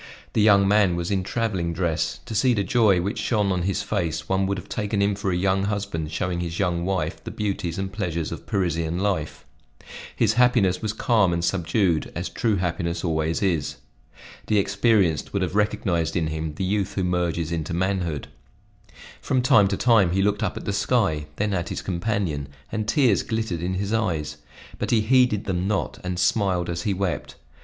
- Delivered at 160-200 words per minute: Yes, average, 195 wpm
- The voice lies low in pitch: Yes, very low, 95 Hz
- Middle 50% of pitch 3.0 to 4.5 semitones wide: Yes, average, 3.3 semitones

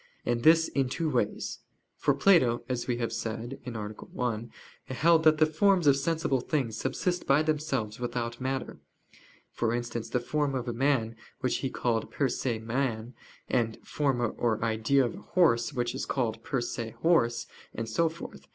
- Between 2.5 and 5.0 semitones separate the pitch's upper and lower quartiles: Yes, average, 3.8 semitones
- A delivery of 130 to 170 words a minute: No, average, 180 wpm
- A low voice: Yes, low, 125 Hz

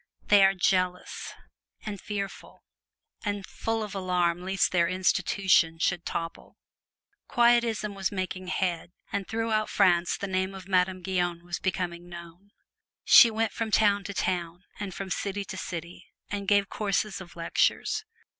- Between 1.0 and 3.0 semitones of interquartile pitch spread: Yes, narrow, 2.4 semitones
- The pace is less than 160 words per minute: Yes, average, 145 wpm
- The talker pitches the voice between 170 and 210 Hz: Yes, high, 190 Hz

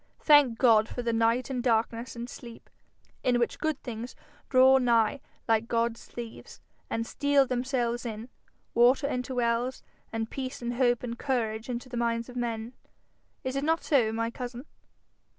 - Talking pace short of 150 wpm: No, average, 165 wpm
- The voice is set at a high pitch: Yes, high, 240 Hz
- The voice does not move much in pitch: Yes, narrow, 1.8 semitones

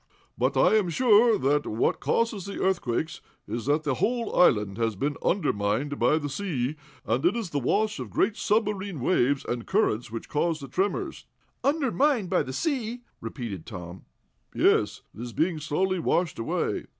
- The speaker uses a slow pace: No, average, 170 wpm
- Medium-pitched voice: Yes, medium, 160 Hz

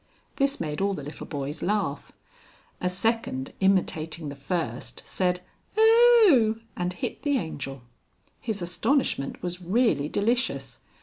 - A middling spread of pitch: No, wide, 7.3 semitones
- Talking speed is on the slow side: Yes, slow, 125 wpm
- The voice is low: No, medium, 180 Hz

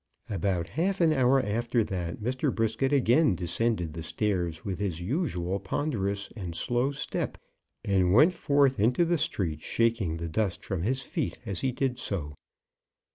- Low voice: Yes, low, 110 Hz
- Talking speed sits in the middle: Yes, average, 160 wpm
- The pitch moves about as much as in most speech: No, wide, 6.6 semitones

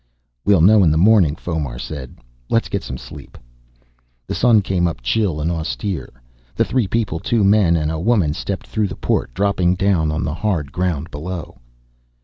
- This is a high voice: No, very low, 85 Hz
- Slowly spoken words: No, average, 180 wpm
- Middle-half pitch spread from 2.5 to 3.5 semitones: No, average, 4.6 semitones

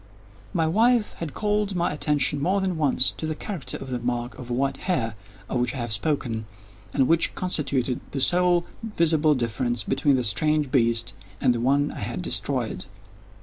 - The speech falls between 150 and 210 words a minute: Yes, average, 180 wpm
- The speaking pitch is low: No, medium, 145 Hz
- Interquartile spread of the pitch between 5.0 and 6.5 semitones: Yes, wide, 5.6 semitones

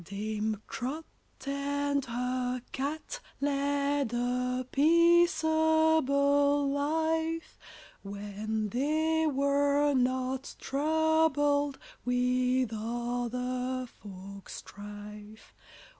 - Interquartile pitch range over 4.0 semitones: No, average, 3.1 semitones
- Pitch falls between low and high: No, very high, 275 Hz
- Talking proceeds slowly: Yes, slow, 70 wpm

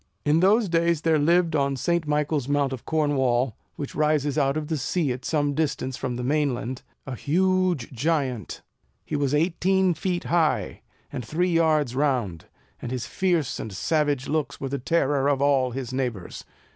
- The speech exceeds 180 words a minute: No, average, 175 wpm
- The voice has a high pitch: No, medium, 145 Hz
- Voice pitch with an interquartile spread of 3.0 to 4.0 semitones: Yes, average, 3.7 semitones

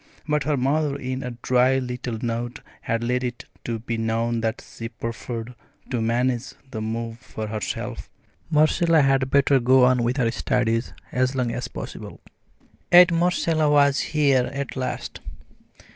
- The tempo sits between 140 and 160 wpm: Yes, average, 150 wpm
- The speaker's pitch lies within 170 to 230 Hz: No, low, 125 Hz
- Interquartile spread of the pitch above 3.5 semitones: No, average, 3.0 semitones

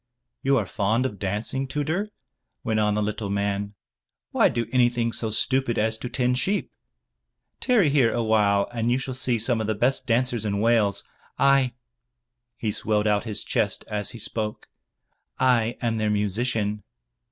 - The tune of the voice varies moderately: Yes, average, 3.1 semitones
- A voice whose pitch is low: Yes, low, 115 Hz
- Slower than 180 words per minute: Yes, average, 165 wpm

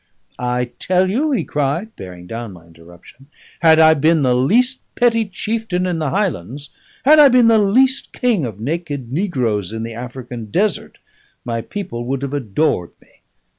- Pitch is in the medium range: Yes, medium, 145 Hz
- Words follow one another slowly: No, average, 170 wpm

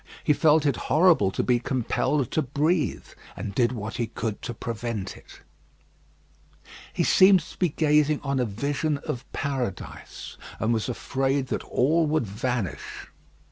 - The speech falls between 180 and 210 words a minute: No, average, 150 wpm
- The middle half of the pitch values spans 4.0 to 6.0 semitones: Yes, average, 4.4 semitones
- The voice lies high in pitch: No, low, 135 Hz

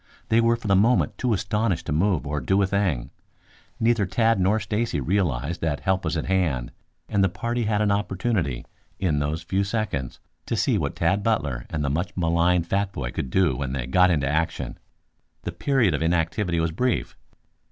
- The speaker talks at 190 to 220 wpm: Yes, average, 195 wpm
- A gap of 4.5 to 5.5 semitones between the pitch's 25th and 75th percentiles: Yes, average, 5.2 semitones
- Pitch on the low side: Yes, very low, 90 Hz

